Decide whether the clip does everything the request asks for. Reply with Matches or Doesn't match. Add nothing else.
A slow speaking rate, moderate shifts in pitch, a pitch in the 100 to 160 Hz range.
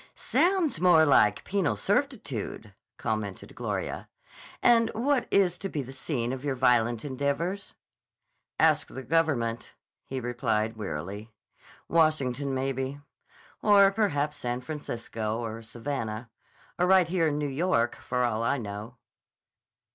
Doesn't match